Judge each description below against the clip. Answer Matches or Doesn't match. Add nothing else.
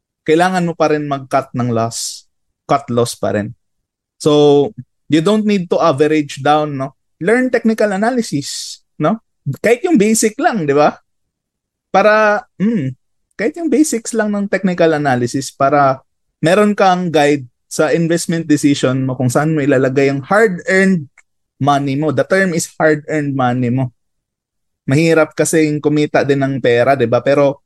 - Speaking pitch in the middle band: Matches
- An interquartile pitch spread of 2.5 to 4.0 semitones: Doesn't match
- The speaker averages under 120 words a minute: Doesn't match